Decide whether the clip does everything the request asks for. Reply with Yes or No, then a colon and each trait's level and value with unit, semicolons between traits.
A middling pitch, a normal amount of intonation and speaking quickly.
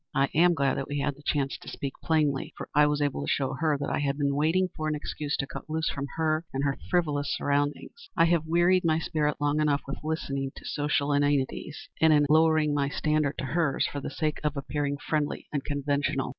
No: medium, 145 Hz; narrow, 1.8 semitones; fast, 225 wpm